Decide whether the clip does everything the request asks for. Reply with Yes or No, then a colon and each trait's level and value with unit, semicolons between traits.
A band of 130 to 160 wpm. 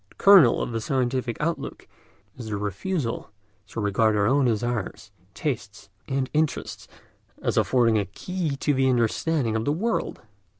Yes: average, 155 wpm